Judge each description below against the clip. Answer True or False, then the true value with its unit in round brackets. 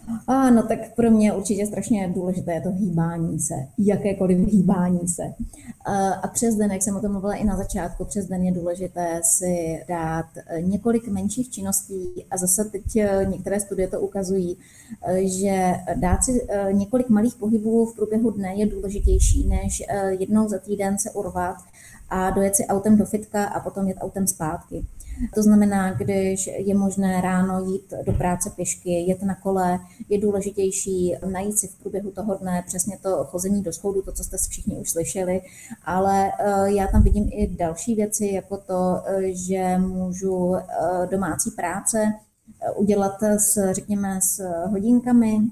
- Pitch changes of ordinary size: False (2.1 semitones)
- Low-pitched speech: False (195 Hz)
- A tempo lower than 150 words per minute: False (155 wpm)